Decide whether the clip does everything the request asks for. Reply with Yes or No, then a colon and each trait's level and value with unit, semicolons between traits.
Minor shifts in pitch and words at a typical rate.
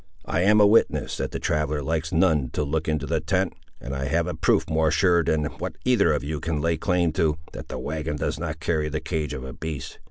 No: narrow, 1.7 semitones; fast, 245 wpm